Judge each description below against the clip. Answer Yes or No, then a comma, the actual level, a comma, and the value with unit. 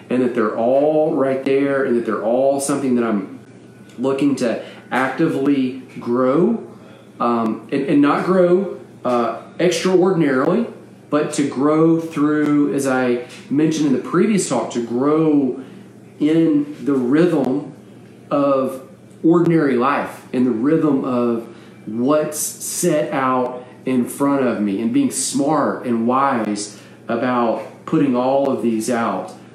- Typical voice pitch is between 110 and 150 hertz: Yes, low, 135 Hz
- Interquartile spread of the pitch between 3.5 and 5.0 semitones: Yes, average, 3.9 semitones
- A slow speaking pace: Yes, slow, 130 wpm